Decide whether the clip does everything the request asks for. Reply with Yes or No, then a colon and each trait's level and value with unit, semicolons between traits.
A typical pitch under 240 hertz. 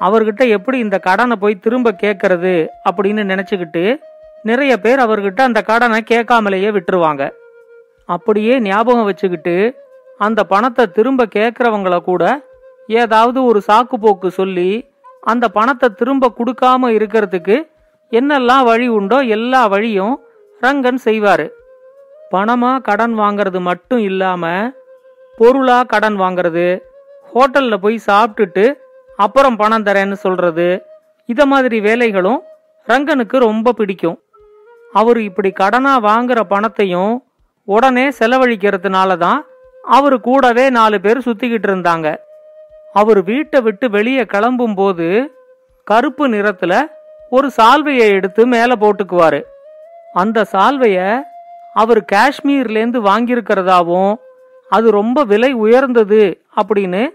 Yes: high, 230 Hz